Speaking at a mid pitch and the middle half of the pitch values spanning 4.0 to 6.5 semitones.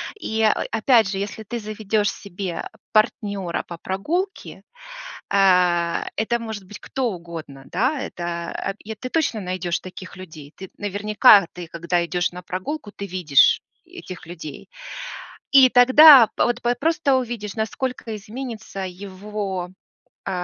No: high, 200 Hz; average, 4.4 semitones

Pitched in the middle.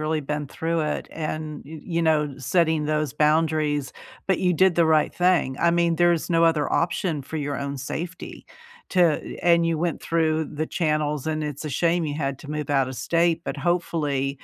Yes: medium, 155 Hz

